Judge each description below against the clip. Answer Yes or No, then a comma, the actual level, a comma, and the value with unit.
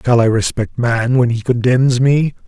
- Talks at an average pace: Yes, average, 195 wpm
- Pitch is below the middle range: Yes, low, 120 Hz